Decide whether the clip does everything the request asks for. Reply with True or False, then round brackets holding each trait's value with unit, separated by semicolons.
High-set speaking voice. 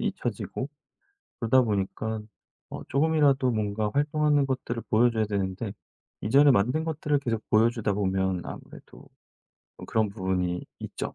False (115 Hz)